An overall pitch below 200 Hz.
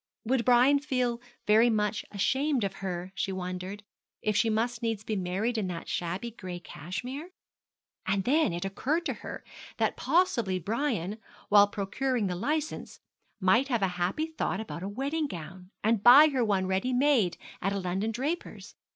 No: high, 215 Hz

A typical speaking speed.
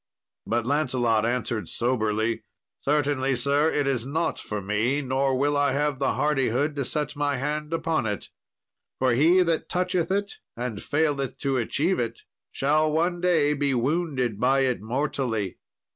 Yes: average, 155 wpm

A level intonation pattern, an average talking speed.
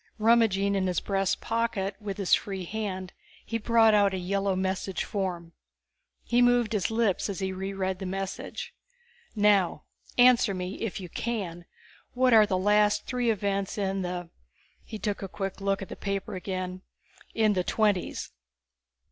Yes: narrow, 2.3 semitones; average, 165 wpm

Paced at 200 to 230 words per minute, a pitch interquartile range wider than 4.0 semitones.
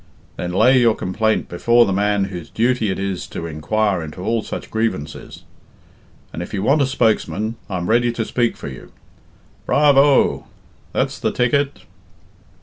No: average, 155 wpm; average, 4.4 semitones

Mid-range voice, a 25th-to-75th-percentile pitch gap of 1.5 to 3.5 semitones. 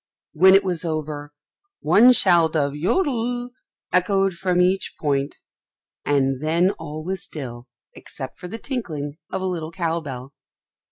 No: medium, 170 Hz; average, 4.5 semitones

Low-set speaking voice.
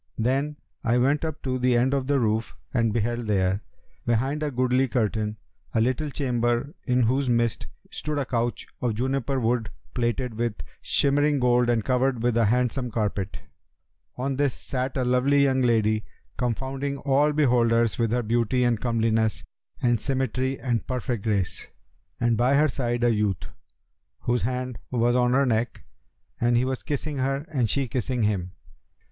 Yes: low, 125 Hz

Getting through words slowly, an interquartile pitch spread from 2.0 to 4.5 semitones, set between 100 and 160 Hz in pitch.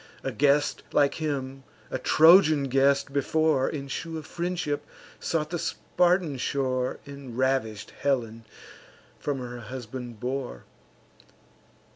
Yes: slow, 115 wpm; average, 3.0 semitones; medium, 140 Hz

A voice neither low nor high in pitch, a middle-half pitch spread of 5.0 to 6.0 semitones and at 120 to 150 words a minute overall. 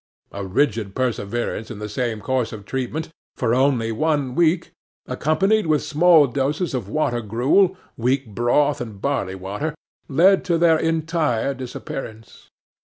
No: low, 130 Hz; wide, 5.6 semitones; average, 140 wpm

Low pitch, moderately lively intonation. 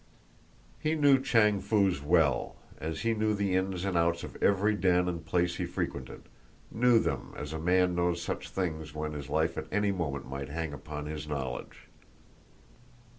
Yes: very low, 85 Hz; average, 4.6 semitones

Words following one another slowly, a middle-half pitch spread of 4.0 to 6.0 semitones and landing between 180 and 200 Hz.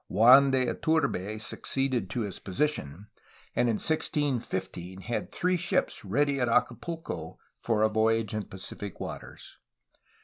No: slow, 130 wpm; average, 5.2 semitones; low, 115 Hz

